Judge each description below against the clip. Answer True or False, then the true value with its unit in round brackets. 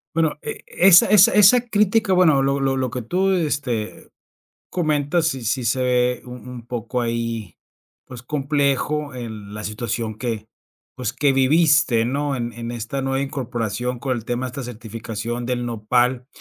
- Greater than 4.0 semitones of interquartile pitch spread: False (3.5 semitones)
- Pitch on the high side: False (125 Hz)